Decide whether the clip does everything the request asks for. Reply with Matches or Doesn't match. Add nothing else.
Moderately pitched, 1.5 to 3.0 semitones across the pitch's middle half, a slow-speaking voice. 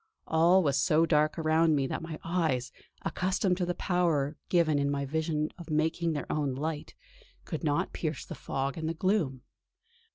Doesn't match